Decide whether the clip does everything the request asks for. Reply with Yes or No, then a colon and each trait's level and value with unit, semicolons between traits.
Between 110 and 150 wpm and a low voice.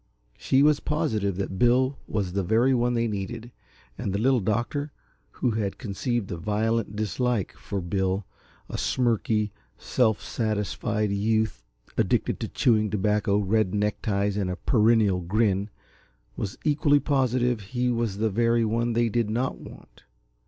Yes: average, 145 wpm; low, 110 Hz